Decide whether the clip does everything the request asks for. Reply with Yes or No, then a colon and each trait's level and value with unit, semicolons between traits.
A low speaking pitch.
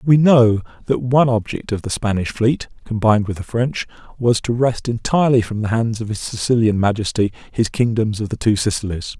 Yes: low, 115 Hz